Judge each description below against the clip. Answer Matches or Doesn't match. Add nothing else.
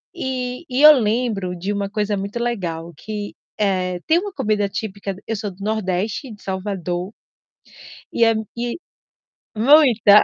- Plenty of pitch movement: Doesn't match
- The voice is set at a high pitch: Matches